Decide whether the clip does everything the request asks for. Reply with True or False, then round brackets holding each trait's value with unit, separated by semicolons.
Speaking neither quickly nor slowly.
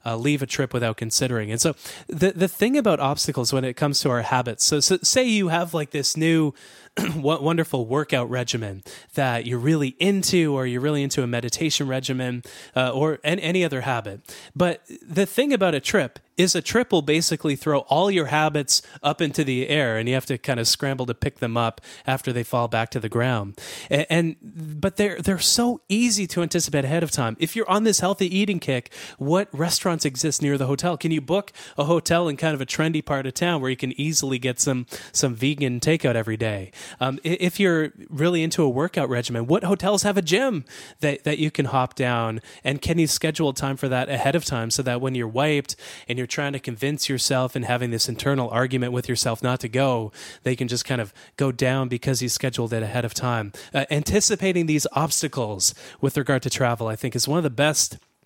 False (220 wpm)